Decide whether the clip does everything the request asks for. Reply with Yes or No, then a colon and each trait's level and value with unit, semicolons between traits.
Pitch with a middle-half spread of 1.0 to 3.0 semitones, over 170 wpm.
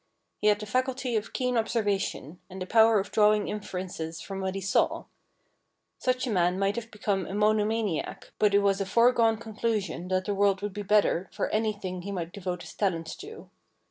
Yes: average, 2.7 semitones; average, 200 wpm